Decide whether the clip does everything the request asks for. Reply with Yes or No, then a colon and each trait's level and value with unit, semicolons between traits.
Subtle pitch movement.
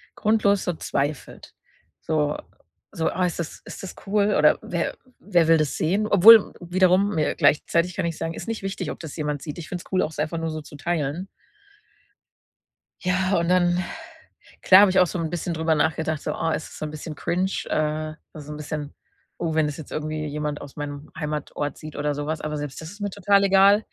No: average, 3.5 semitones